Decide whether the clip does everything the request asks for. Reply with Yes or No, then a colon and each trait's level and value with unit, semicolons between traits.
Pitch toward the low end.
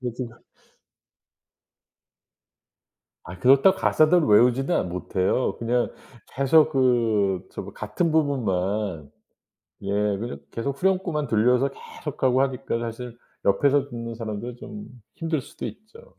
Yes: low, 125 Hz